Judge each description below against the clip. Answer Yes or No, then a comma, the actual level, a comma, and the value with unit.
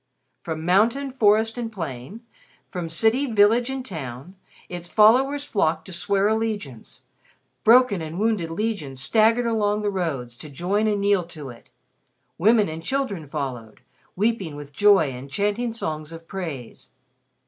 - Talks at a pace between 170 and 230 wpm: No, average, 145 wpm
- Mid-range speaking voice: No, high, 195 Hz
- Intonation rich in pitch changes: Yes, wide, 6.0 semitones